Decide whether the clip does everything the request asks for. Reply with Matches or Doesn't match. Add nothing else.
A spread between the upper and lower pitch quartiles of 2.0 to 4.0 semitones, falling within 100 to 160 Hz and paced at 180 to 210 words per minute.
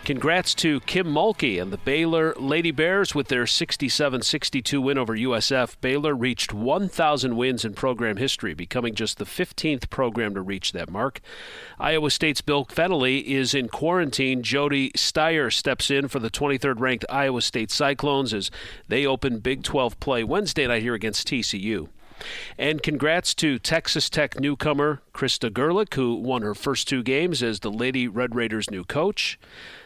Doesn't match